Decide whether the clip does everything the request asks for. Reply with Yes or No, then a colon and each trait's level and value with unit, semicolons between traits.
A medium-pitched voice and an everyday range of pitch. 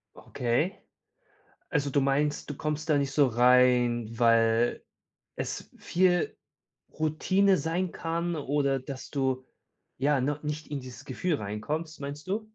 Yes: medium, 145 Hz; average, 3.7 semitones